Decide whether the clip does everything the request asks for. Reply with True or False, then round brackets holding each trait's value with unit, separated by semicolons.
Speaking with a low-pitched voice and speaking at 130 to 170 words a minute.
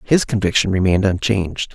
True (100 Hz; 135 wpm)